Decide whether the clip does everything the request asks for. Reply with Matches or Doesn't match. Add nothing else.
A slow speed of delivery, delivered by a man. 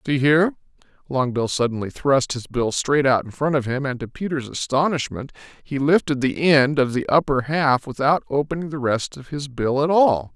Doesn't match